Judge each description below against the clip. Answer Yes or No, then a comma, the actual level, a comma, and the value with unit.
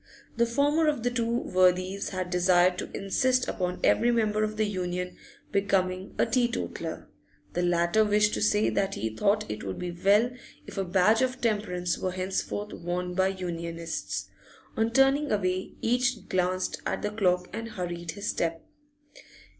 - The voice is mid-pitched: No, high, 195 Hz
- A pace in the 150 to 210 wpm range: Yes, average, 160 wpm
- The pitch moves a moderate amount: Yes, average, 3.7 semitones